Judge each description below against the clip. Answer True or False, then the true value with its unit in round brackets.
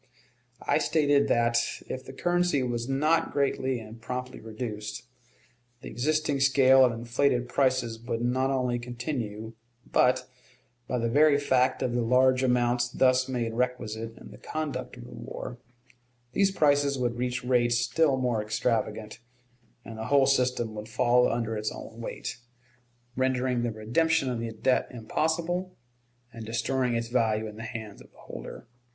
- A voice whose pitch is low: True (125 Hz)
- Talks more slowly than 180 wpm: True (155 wpm)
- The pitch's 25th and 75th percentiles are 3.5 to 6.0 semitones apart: False (2.5 semitones)